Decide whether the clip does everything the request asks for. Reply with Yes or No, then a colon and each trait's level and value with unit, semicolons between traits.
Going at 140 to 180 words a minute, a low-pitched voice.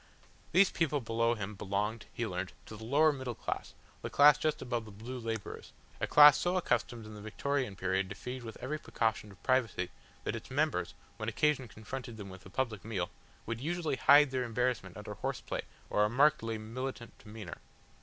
No: average, 190 wpm; low, 115 Hz